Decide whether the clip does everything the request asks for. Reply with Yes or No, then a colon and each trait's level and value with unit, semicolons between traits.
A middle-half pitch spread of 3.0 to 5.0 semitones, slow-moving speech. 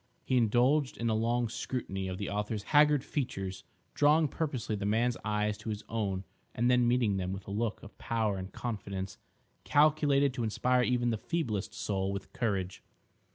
No: average, 3.9 semitones; average, 175 wpm